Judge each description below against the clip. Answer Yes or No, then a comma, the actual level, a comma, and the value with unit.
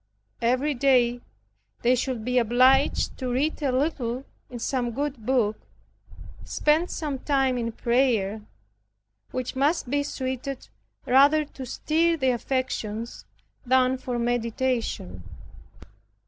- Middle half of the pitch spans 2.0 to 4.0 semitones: Yes, narrow, 2.4 semitones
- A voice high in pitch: Yes, very high, 255 Hz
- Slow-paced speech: Yes, slow, 115 wpm